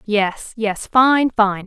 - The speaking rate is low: Yes, slow, 110 wpm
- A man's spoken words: No, female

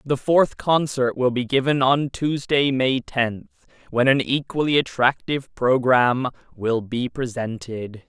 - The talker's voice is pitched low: Yes, low, 130 Hz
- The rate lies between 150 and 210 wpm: No, slow, 135 wpm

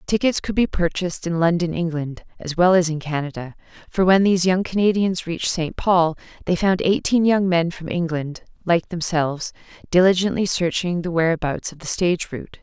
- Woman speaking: Yes, female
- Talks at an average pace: Yes, average, 175 wpm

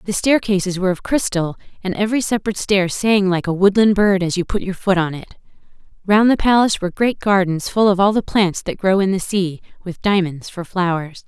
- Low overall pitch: No, high, 190 Hz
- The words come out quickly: Yes, fast, 220 wpm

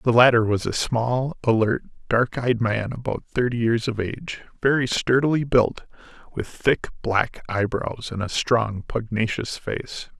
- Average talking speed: Yes, average, 155 wpm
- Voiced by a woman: No, male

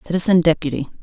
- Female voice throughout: Yes, female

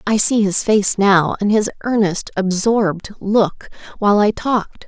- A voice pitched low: No, high, 205 Hz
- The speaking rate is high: No, average, 160 wpm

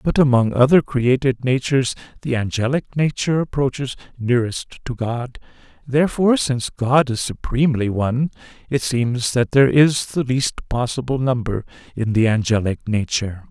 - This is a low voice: Yes, low, 125 Hz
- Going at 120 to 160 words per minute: Yes, average, 140 wpm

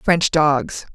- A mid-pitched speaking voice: Yes, medium, 155 Hz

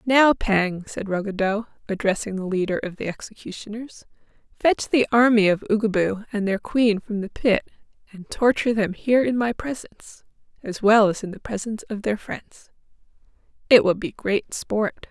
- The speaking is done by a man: No, female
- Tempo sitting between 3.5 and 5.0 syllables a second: Yes, 4.9 syllables/s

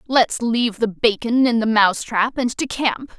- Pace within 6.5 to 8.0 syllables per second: No, 4.6 syllables/s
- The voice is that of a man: No, female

